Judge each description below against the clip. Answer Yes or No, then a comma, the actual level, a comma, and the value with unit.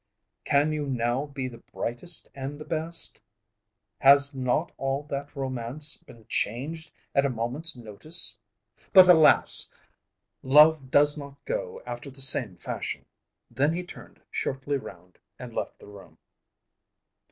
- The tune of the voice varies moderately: Yes, average, 3.5 semitones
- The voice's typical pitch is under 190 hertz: Yes, medium, 140 Hz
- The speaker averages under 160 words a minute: Yes, slow, 135 wpm